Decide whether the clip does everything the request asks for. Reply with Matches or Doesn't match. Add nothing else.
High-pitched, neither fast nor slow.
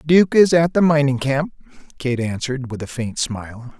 Doesn't match